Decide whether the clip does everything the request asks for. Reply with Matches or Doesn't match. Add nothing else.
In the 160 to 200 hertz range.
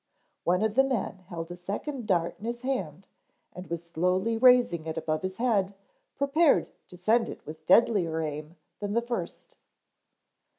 Matches